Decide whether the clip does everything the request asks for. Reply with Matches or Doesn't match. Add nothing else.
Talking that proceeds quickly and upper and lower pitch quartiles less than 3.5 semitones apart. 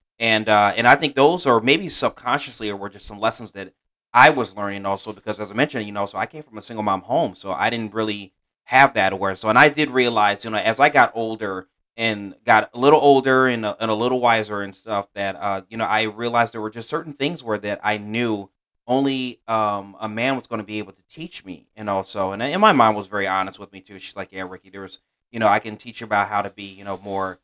Matches